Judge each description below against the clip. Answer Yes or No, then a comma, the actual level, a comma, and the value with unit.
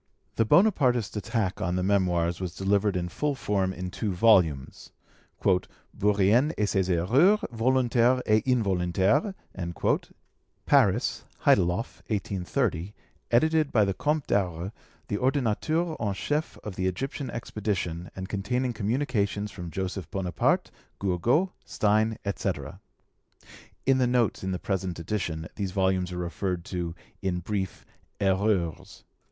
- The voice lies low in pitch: Yes, low, 100 Hz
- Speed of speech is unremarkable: No, slow, 125 wpm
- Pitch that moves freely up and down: No, average, 4.6 semitones